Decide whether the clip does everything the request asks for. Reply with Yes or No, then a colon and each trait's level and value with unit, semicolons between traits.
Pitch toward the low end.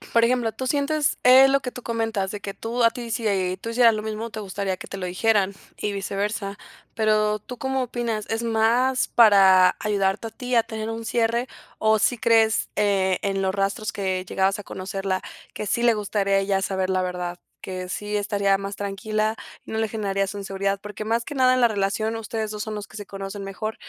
No: high, 210 Hz